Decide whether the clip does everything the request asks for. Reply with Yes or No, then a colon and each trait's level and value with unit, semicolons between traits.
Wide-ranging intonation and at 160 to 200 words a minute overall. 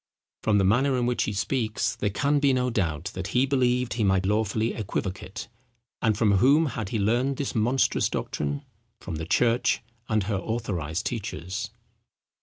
No: average, 4.3 semitones; average, 170 wpm